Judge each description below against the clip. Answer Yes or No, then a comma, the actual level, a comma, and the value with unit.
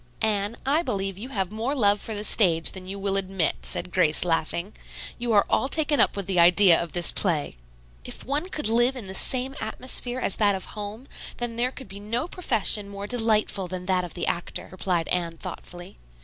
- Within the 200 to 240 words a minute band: Yes, fast, 205 wpm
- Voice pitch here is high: Yes, high, 200 Hz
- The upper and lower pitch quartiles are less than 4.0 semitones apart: No, average, 4.5 semitones